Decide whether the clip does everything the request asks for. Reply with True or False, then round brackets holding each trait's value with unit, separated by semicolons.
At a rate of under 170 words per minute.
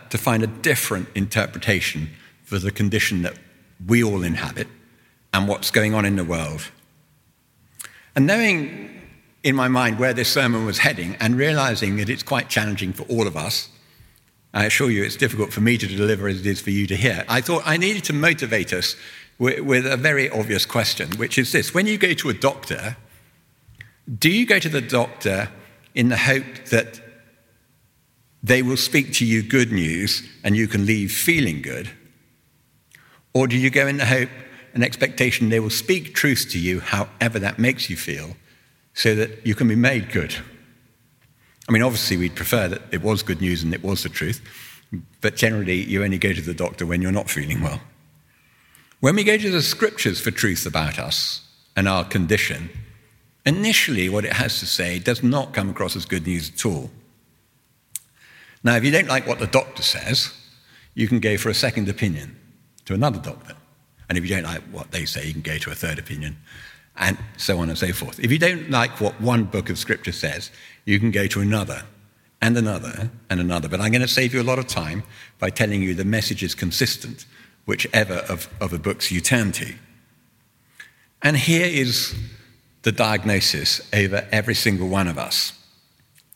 False (190 wpm)